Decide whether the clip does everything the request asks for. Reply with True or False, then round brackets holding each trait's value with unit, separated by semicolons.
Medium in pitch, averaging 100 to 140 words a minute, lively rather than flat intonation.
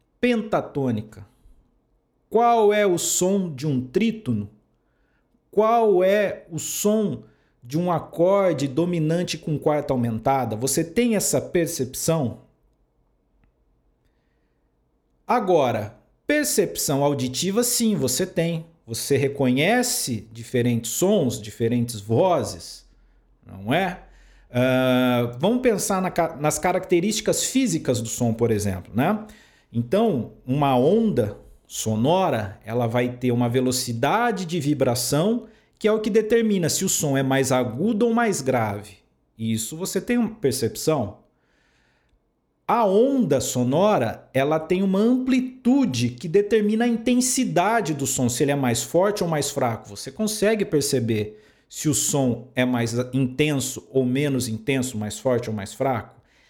True (145 Hz; 125 wpm; 8.5 semitones)